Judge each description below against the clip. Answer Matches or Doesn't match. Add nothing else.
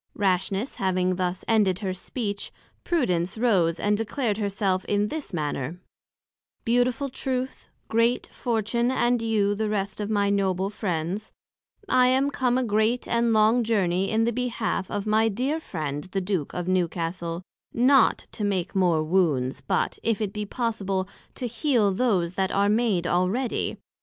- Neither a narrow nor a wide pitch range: Matches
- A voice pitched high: Matches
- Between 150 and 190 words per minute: Matches